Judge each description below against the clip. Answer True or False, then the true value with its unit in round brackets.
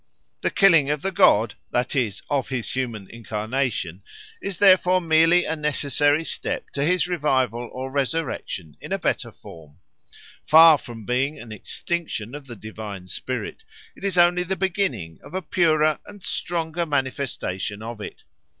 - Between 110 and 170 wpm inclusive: True (155 wpm)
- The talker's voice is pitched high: False (140 Hz)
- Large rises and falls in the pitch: True (6.5 semitones)